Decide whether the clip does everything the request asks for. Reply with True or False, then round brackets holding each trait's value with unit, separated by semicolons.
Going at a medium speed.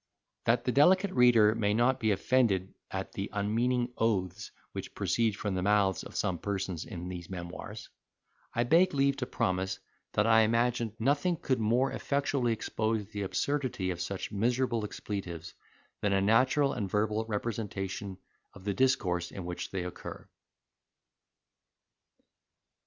True (145 wpm)